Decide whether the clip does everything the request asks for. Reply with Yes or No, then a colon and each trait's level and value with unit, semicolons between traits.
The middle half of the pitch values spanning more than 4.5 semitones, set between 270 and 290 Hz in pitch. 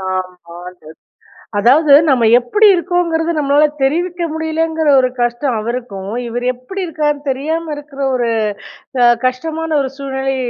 Yes: average, 5.0 semitones; very high, 280 Hz